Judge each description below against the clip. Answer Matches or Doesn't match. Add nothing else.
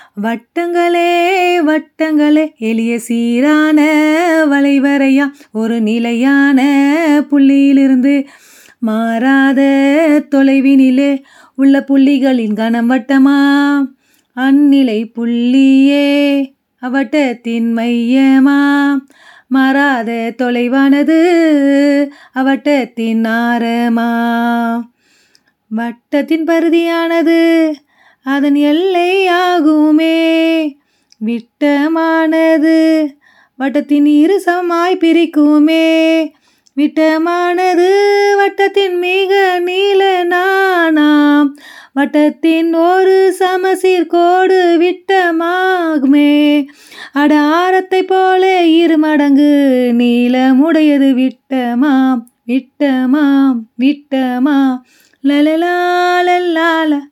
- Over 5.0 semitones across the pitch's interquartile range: Doesn't match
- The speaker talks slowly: Matches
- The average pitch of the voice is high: Matches